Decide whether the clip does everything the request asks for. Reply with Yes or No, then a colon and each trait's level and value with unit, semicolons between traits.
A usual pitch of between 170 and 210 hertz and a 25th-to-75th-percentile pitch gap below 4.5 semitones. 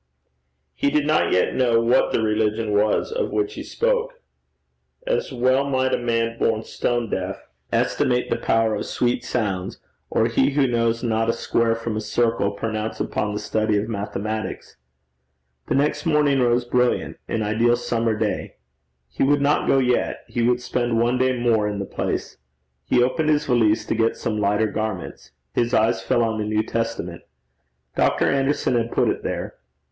No: low, 115 Hz; average, 2.7 semitones